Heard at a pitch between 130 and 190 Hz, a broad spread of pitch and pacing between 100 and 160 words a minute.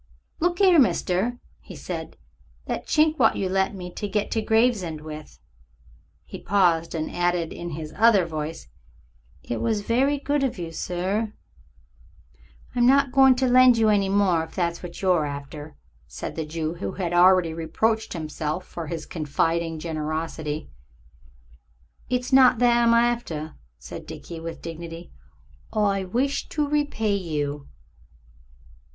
Yes: medium, 185 Hz; wide, 6.2 semitones; average, 145 wpm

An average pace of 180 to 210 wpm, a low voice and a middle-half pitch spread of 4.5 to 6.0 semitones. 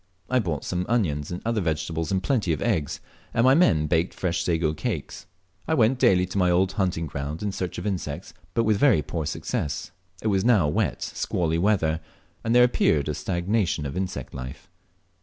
Yes: average, 195 wpm; very low, 90 Hz; average, 4.9 semitones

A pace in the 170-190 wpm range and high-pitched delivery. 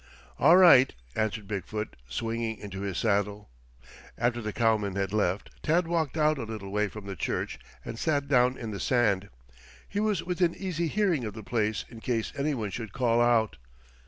No: average, 185 wpm; low, 115 Hz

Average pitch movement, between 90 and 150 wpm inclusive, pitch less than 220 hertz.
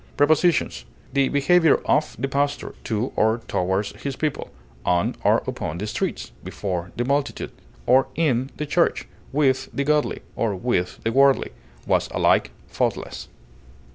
Yes: average, 5.0 semitones; average, 140 wpm; low, 135 Hz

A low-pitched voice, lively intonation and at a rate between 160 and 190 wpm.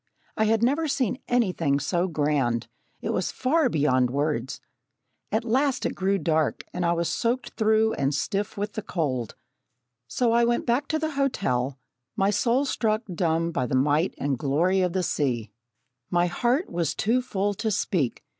No: high, 190 Hz; wide, 8.2 semitones; average, 175 wpm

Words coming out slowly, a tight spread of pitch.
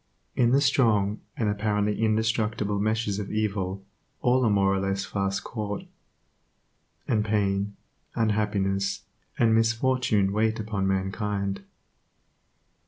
Yes: slow, 110 wpm; narrow, 2.2 semitones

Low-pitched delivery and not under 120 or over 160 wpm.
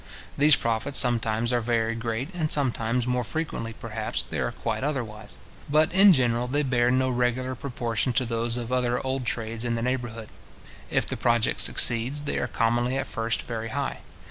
No: low, 120 Hz; average, 180 wpm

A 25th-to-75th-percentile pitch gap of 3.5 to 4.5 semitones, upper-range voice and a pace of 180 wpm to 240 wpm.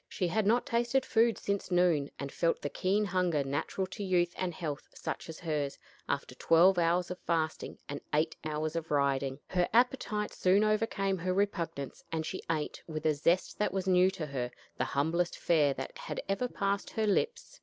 No: average, 4.2 semitones; medium, 175 Hz; average, 190 wpm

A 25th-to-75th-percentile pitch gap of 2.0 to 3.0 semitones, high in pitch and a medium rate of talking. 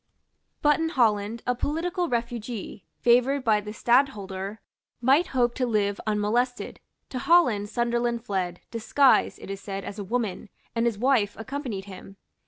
No: average, 3.7 semitones; high, 235 Hz; average, 150 wpm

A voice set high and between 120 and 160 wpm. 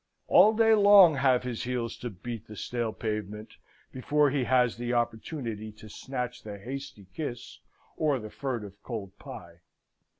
No: low, 120 Hz; average, 155 wpm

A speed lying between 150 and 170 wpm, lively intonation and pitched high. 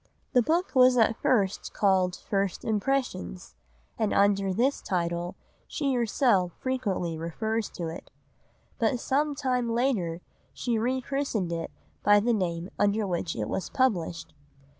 No: average, 140 wpm; wide, 5.8 semitones; high, 210 Hz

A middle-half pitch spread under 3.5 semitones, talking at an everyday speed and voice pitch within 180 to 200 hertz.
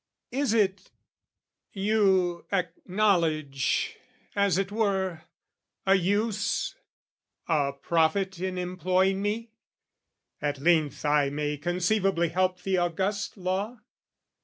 No: average, 3.0 semitones; slow, 95 wpm; medium, 185 Hz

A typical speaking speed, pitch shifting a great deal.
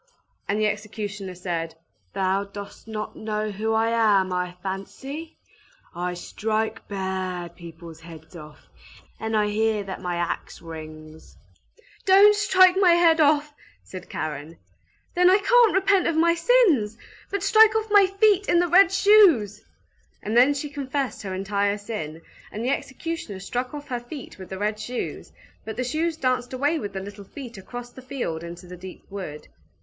Yes: average, 165 wpm; wide, 8.5 semitones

